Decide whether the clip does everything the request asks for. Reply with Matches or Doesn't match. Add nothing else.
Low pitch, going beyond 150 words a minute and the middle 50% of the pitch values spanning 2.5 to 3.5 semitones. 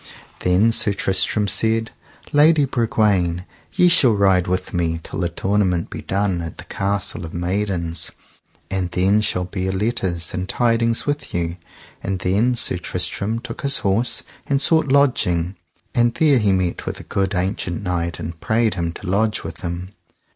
Doesn't match